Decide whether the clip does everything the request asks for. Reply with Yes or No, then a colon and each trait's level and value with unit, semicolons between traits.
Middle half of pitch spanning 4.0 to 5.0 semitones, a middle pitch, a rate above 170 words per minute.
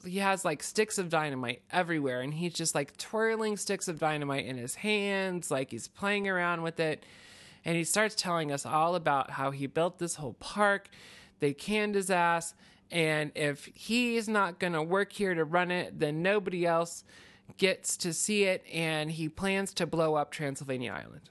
Yes: average, 4.4 semitones; medium, 170 Hz; average, 185 wpm